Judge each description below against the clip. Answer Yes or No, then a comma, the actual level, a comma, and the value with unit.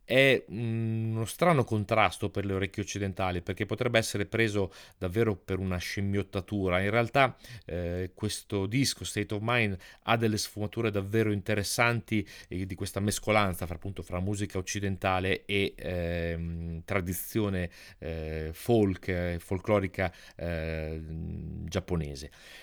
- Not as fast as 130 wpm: Yes, average, 120 wpm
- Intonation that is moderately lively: Yes, average, 3.1 semitones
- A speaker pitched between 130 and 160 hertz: No, low, 100 Hz